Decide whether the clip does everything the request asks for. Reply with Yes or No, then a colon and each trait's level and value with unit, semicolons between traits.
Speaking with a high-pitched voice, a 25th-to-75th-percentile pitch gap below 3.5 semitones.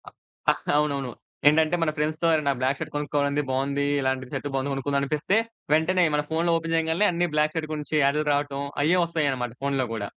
No: medium, 150 Hz; narrow, 2.5 semitones